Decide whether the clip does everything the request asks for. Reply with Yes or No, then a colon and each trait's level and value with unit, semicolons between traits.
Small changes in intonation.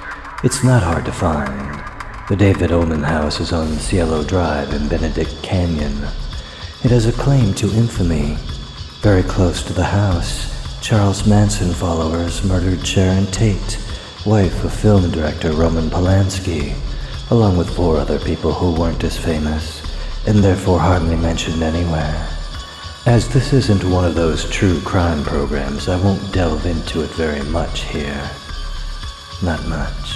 No: average, 3.8 semitones